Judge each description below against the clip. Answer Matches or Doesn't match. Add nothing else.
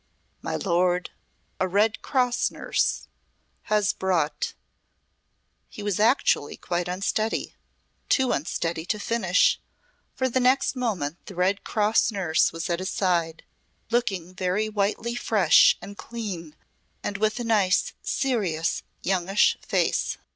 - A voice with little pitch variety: Doesn't match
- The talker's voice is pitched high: Matches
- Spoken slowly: Matches